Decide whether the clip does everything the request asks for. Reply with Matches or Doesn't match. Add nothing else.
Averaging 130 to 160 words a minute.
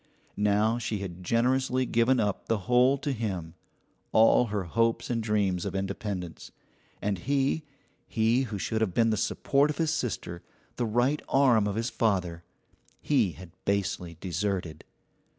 Matches